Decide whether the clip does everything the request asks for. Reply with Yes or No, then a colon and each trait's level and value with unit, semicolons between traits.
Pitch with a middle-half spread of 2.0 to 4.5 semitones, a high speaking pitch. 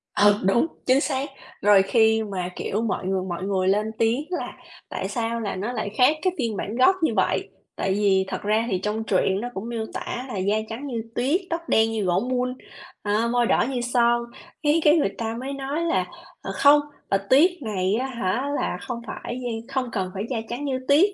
Yes: average, 4.2 semitones; high, 230 Hz